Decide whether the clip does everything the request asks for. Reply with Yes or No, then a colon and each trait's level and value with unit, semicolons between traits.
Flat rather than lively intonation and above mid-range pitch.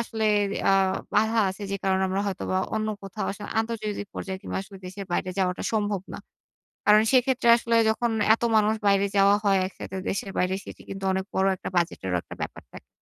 Yes: narrow, 2.3 semitones; high, 200 Hz